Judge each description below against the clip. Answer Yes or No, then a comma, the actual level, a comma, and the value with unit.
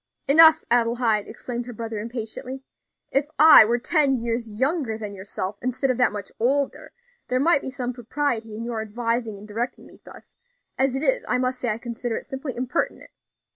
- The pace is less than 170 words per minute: No, average, 185 wpm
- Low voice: No, high, 245 Hz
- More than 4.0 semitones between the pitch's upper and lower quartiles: No, average, 2.9 semitones